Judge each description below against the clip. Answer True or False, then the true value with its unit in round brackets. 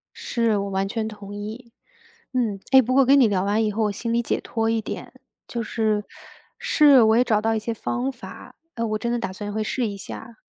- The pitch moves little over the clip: True (2.3 semitones)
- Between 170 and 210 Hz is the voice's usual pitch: False (225 Hz)